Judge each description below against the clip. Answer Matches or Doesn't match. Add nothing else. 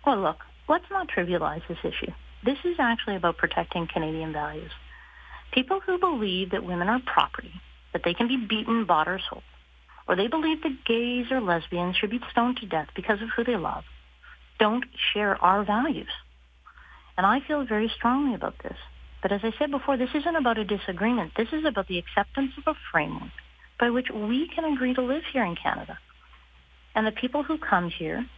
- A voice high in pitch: Matches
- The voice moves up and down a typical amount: Doesn't match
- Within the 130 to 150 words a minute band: Doesn't match